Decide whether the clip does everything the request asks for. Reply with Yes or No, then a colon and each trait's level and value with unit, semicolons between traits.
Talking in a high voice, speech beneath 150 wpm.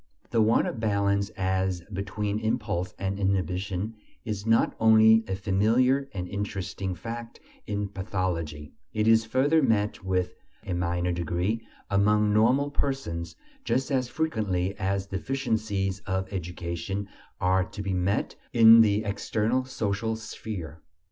No: low, 100 Hz; average, 140 wpm